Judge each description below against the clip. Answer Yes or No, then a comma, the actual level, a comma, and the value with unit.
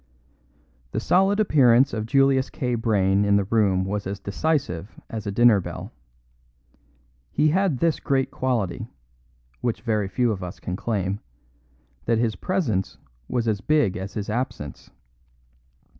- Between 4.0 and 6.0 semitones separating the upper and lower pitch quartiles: Yes, average, 5.0 semitones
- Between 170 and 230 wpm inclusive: No, average, 145 wpm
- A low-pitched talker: Yes, low, 110 Hz